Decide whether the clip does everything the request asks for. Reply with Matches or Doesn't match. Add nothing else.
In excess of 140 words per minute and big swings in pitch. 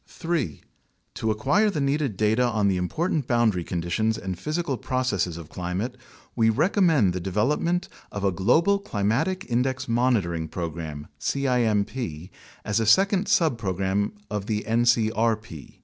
Doesn't match